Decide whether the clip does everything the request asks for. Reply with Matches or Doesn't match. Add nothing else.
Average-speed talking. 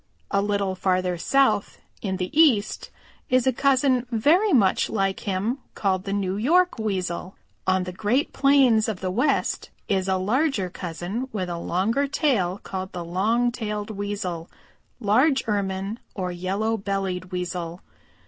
Matches